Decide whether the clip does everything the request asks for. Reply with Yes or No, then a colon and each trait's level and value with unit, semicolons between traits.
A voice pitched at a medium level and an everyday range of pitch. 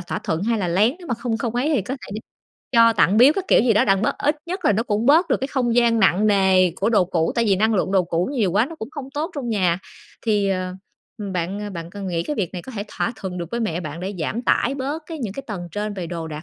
No: high, 210 Hz; average, 4.8 semitones